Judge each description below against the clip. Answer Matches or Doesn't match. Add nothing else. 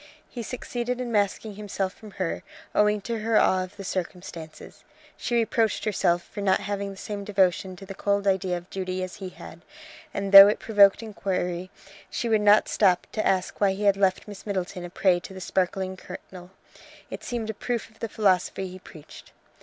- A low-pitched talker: Doesn't match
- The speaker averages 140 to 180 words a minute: Doesn't match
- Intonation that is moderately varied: Doesn't match